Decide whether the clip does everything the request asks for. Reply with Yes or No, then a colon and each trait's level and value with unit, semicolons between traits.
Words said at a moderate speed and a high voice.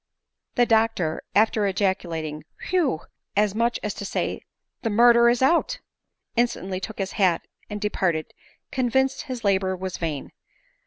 Yes: average, 160 wpm; high, 210 Hz